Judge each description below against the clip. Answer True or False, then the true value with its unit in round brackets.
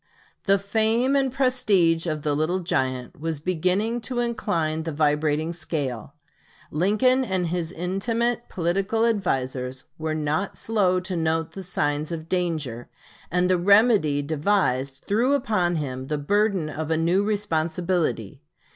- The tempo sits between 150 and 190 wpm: False (140 wpm)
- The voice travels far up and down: False (5.0 semitones)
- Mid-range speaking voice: True (175 Hz)